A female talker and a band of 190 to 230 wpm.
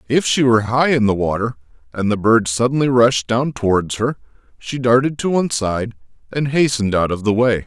No: male; fast, 205 wpm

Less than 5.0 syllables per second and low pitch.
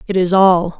No: 4.8 syllables/s; medium, 185 Hz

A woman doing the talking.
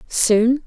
Yes: female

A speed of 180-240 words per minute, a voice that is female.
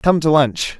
No: fast, 230 wpm; male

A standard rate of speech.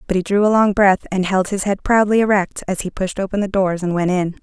No: fast, 285 wpm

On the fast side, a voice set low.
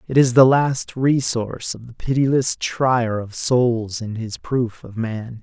No: average, 175 wpm; low, 120 Hz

